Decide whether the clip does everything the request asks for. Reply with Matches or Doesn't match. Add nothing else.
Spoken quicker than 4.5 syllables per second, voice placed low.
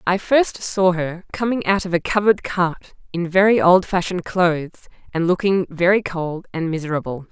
Doesn't match